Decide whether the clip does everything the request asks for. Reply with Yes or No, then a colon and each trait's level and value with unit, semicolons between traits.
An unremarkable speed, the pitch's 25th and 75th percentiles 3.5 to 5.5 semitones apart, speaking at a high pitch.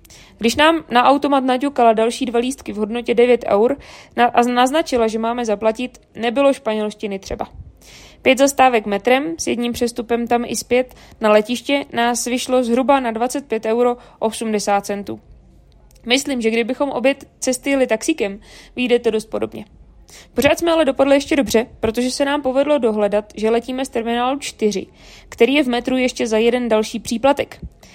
No: average, 160 wpm; average, 2.9 semitones; high, 240 Hz